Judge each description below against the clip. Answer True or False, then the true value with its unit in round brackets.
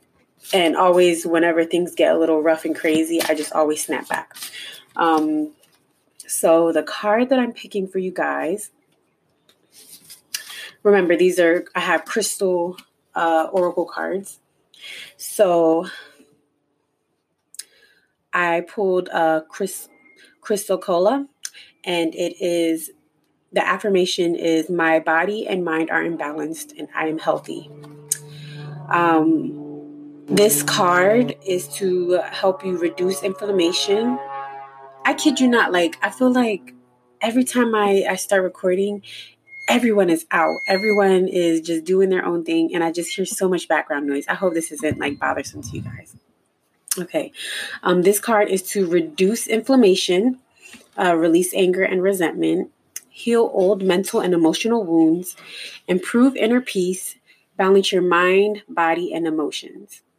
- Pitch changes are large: False (3.5 semitones)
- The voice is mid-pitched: True (180 Hz)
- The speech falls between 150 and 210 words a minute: False (135 wpm)